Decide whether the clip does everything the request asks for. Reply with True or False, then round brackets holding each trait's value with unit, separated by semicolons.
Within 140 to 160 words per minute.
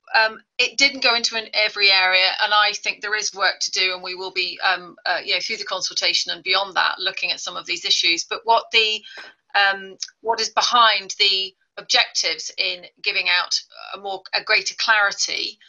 False (205 wpm)